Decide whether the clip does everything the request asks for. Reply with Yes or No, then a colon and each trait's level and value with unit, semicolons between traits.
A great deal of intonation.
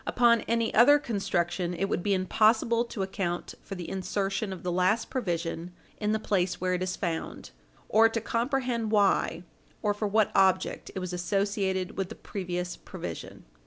No: average, 3.5 semitones